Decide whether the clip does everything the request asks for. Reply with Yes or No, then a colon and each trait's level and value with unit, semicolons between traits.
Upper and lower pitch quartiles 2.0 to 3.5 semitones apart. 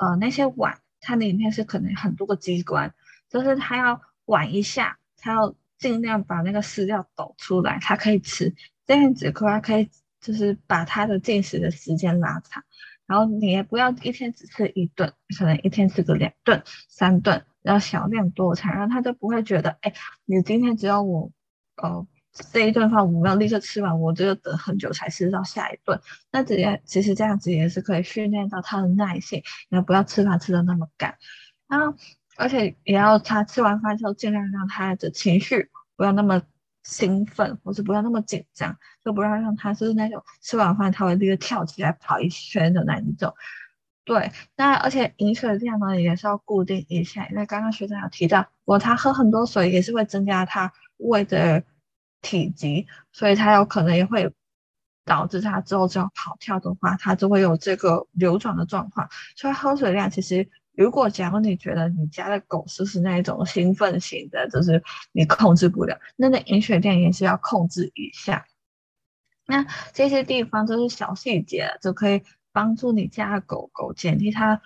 Yes: average, 2.9 semitones